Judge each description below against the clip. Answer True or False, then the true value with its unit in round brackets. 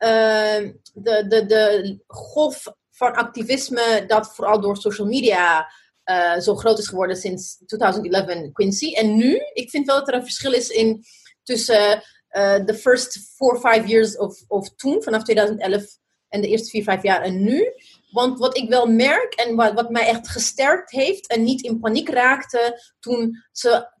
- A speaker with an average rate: True (180 wpm)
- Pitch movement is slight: False (3.1 semitones)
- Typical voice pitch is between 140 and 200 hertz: False (225 Hz)